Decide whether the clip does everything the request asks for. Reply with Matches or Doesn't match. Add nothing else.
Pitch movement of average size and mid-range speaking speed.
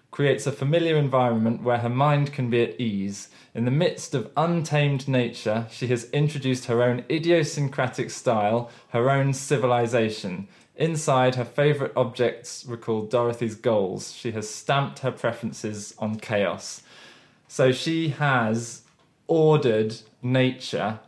Doesn't match